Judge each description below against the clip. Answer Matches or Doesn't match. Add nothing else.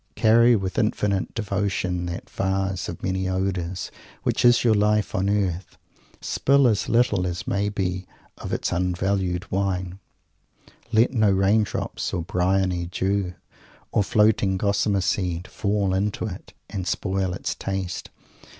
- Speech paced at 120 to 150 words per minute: Matches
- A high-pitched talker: Doesn't match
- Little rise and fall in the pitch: Matches